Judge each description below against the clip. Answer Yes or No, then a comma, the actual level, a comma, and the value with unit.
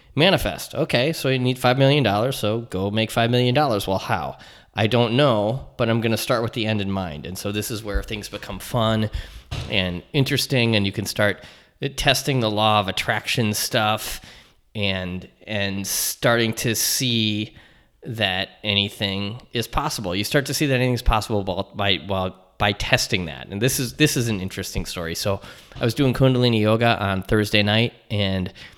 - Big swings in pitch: No, average, 3.6 semitones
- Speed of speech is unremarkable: Yes, average, 180 wpm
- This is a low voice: Yes, low, 110 Hz